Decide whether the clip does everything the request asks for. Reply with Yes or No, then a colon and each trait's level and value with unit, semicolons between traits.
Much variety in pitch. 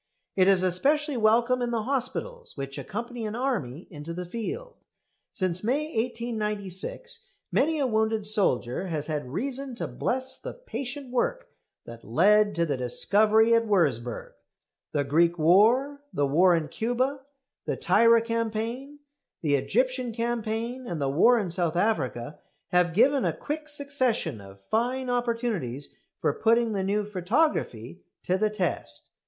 Yes: wide, 6.6 semitones